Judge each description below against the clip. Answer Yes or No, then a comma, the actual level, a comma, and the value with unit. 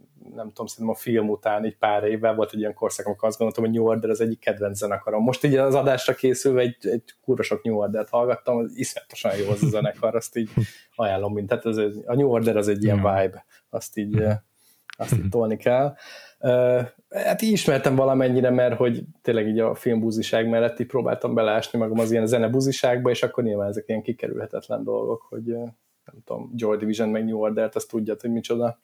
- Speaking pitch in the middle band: No, low, 115 Hz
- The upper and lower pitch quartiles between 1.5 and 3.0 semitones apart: Yes, narrow, 2.4 semitones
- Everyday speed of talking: No, fast, 200 wpm